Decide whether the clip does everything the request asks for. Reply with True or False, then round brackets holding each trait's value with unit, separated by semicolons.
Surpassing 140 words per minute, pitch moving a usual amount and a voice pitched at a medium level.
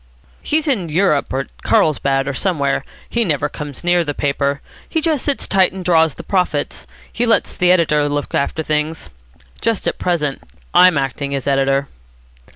True (165 wpm; 4.7 semitones; 155 Hz)